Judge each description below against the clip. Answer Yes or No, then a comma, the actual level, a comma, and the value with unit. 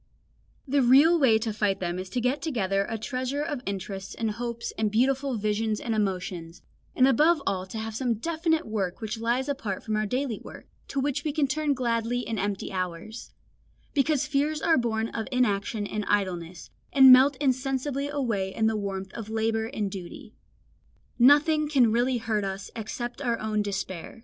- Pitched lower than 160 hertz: No, high, 230 Hz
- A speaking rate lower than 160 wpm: No, average, 180 wpm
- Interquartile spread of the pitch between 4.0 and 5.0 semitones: Yes, average, 4.6 semitones